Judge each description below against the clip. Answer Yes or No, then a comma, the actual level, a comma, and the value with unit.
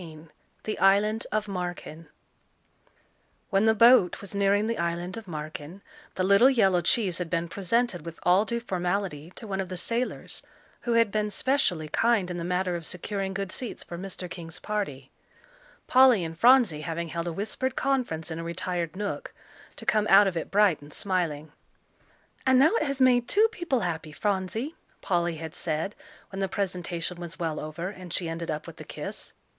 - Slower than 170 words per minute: No, average, 185 wpm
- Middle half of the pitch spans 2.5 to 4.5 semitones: Yes, average, 4.2 semitones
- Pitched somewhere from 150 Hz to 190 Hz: Yes, medium, 185 Hz